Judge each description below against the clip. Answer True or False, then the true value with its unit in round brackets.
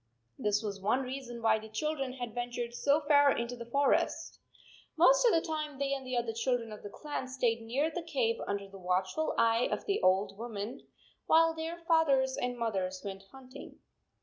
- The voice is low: False (245 Hz)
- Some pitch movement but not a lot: True (4.4 semitones)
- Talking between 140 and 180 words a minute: False (195 wpm)